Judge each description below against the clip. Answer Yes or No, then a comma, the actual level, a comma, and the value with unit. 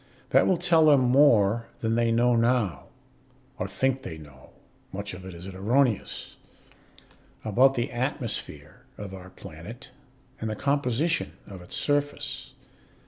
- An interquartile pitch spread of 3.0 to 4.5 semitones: No, wide, 5.5 semitones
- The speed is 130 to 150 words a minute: Yes, average, 140 wpm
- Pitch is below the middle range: Yes, low, 115 Hz